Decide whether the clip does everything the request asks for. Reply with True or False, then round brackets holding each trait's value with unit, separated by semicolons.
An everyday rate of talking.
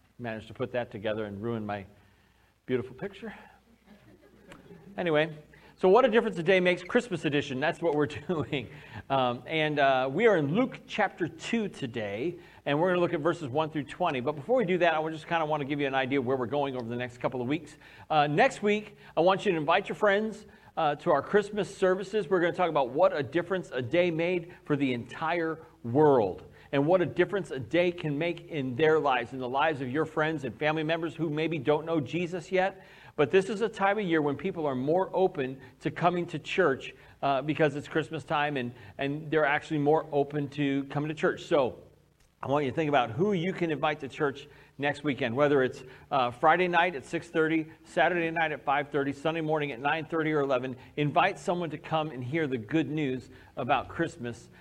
False (220 wpm)